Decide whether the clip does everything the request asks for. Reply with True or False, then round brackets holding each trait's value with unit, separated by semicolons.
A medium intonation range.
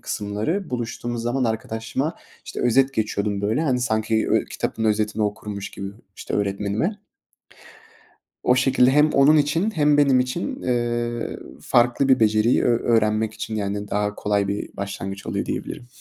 True (4.0 semitones)